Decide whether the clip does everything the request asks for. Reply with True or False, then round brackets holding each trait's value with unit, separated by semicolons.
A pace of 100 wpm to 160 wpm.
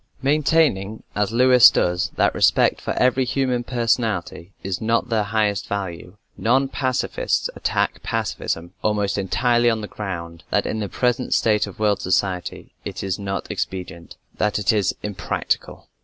True (150 wpm)